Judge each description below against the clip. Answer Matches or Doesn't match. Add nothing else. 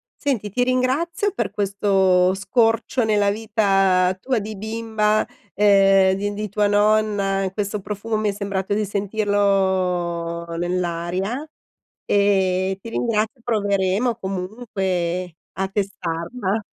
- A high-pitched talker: Matches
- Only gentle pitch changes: Matches